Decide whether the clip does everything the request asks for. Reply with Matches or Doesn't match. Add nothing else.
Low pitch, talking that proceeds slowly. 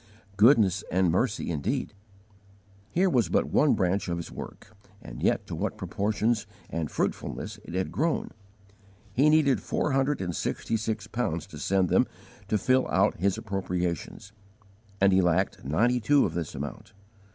Doesn't match